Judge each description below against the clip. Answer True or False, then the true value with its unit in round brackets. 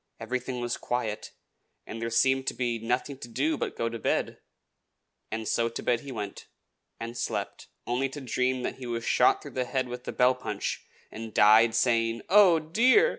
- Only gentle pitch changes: True (2.3 semitones)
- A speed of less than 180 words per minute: False (190 wpm)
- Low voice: True (120 Hz)